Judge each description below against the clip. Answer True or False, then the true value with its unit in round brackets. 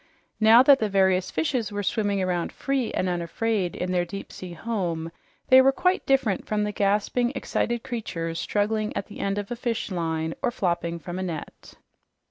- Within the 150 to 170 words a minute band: False (180 wpm)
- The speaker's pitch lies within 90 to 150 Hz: False (205 Hz)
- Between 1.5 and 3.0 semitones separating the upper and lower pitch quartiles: False (4.5 semitones)